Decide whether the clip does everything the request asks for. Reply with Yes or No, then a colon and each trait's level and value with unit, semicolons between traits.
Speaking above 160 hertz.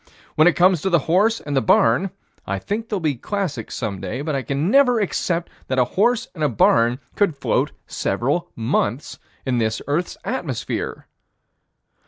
No: medium, 150 Hz